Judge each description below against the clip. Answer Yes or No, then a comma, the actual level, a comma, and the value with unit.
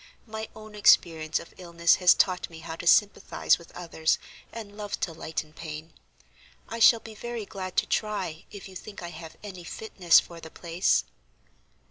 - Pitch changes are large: No, average, 4.1 semitones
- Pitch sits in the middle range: Yes, medium, 180 Hz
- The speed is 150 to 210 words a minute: Yes, average, 175 wpm